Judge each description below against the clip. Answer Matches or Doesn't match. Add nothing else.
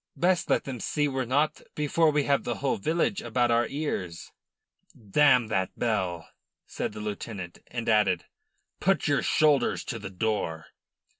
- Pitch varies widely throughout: Matches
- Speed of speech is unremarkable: Matches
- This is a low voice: Matches